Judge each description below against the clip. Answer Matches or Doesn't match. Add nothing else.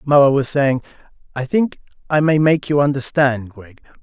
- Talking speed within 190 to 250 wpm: Doesn't match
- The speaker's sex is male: Matches